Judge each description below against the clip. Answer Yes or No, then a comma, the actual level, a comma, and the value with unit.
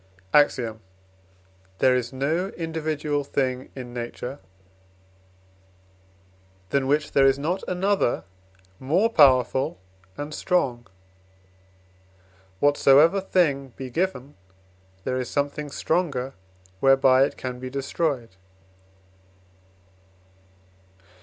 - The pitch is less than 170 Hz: Yes, medium, 140 Hz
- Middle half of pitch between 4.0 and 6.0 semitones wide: No, average, 3.3 semitones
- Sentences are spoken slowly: Yes, slow, 90 wpm